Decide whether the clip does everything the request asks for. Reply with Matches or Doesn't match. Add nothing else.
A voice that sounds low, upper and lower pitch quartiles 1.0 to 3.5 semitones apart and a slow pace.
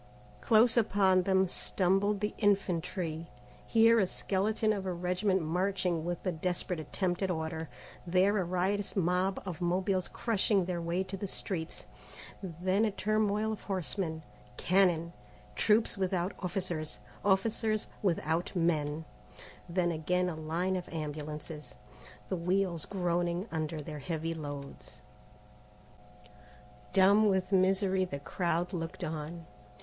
Doesn't match